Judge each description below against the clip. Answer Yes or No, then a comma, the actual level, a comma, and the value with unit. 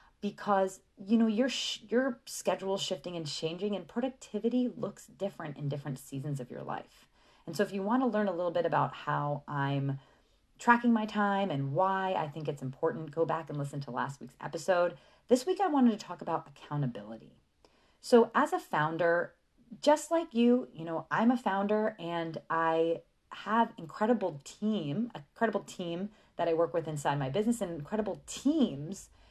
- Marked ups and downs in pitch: Yes, wide, 6.3 semitones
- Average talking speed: Yes, average, 180 wpm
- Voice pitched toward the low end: No, medium, 185 Hz